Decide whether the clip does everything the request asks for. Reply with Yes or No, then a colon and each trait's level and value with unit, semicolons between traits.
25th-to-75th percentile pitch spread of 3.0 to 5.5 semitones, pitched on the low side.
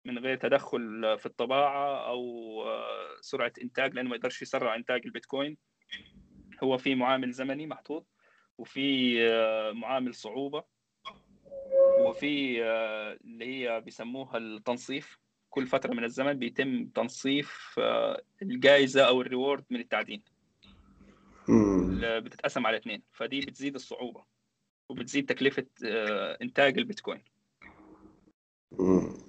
Yes: average, 3.6 semitones; low, 130 Hz